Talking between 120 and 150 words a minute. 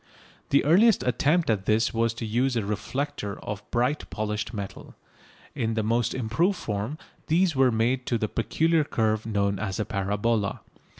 No: average, 165 wpm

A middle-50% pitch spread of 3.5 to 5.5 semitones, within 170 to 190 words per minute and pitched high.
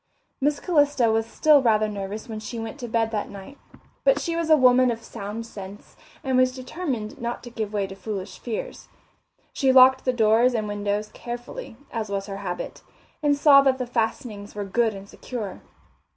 Yes: average, 3.8 semitones; average, 185 wpm; high, 230 Hz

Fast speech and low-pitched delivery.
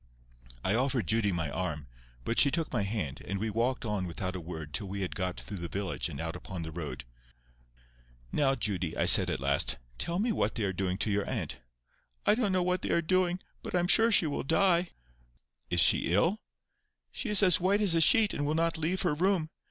Yes: fast, 225 wpm; low, 115 Hz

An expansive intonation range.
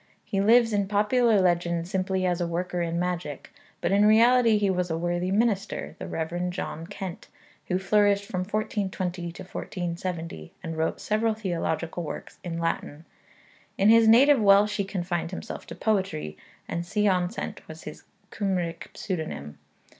No: average, 3.3 semitones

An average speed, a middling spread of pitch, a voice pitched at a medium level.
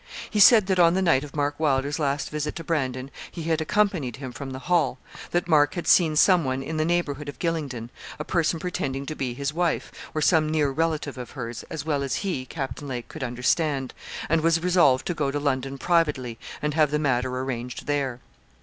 No: fast, 215 wpm; average, 3.7 semitones; medium, 145 Hz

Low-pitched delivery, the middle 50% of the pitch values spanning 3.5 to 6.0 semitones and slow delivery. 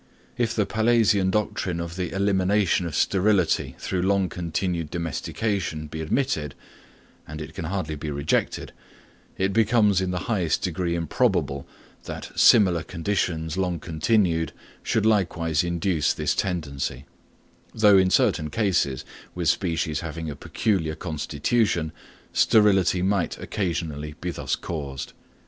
Yes: very low, 90 Hz; average, 3.9 semitones; slow, 125 wpm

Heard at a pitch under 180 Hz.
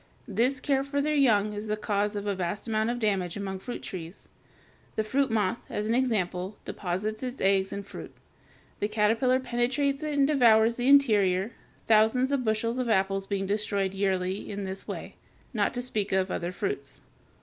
No: high, 215 Hz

